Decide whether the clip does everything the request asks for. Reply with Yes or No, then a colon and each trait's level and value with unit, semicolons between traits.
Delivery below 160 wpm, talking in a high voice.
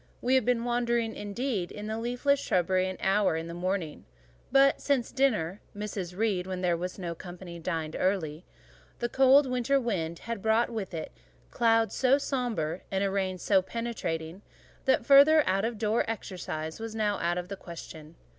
No: average, 170 wpm; high, 205 Hz